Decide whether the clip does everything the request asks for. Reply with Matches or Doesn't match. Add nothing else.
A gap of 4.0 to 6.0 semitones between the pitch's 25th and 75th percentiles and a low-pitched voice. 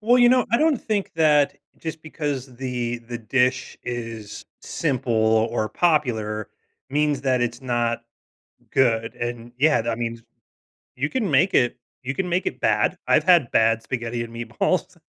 Matches